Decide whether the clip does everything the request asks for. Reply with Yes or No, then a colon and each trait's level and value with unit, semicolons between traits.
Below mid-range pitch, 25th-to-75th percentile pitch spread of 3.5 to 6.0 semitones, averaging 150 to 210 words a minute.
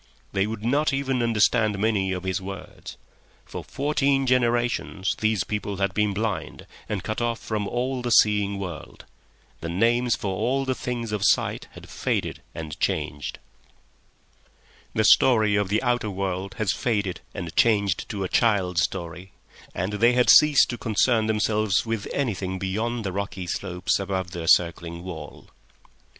Yes: low, 105 Hz; average, 4.0 semitones; average, 155 wpm